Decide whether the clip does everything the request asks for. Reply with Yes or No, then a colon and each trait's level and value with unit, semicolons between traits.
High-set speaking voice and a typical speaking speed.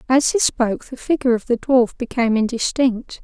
Yes: high, 245 Hz; average, 185 wpm